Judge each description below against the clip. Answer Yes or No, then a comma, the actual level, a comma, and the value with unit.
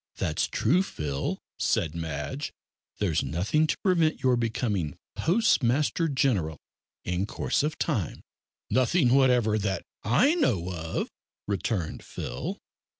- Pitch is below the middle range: Yes, low, 115 Hz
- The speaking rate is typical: No, slow, 115 wpm